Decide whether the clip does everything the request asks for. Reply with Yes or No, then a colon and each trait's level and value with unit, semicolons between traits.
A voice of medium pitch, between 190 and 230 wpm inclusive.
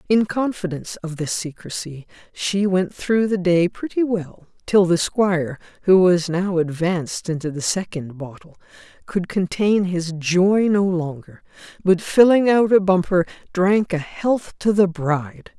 No: medium, 180 Hz; average, 155 wpm